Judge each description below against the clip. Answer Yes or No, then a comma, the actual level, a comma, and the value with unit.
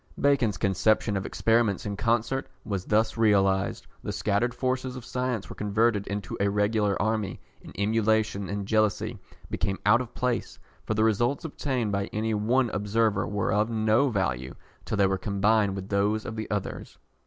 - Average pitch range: No, narrow, 2.3 semitones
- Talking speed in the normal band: Yes, average, 170 wpm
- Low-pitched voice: Yes, low, 105 Hz